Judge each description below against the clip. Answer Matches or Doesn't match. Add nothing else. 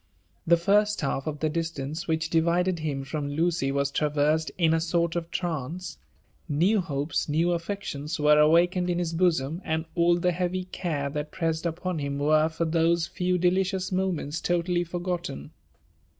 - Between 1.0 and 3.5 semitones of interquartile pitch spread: Matches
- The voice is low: Doesn't match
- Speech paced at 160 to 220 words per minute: Matches